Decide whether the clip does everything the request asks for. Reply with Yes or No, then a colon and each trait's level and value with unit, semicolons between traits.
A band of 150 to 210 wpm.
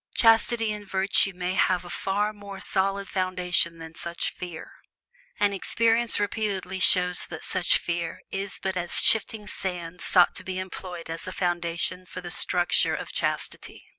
Yes: average, 160 wpm